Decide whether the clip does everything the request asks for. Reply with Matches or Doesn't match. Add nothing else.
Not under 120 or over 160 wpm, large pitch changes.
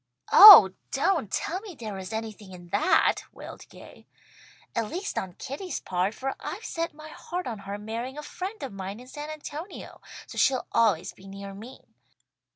Doesn't match